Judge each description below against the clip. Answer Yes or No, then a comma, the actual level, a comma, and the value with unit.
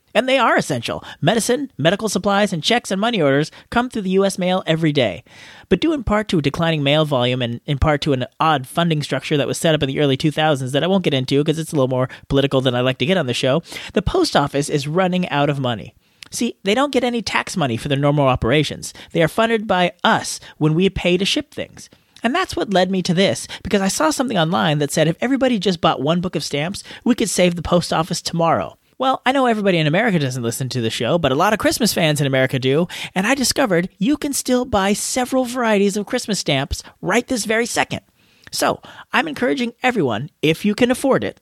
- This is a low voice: No, medium, 175 Hz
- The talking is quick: Yes, fast, 240 wpm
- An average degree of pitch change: No, wide, 7.5 semitones